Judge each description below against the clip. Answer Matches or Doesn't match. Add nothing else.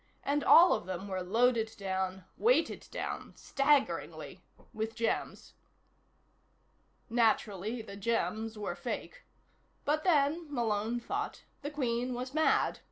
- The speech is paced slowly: Matches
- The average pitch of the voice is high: Matches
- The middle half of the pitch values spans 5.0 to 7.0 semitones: Matches